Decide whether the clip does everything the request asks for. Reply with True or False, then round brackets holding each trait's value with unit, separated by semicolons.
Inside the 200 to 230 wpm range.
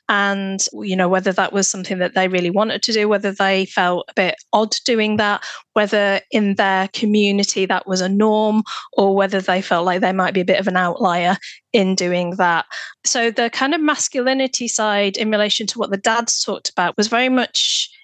True (205 wpm)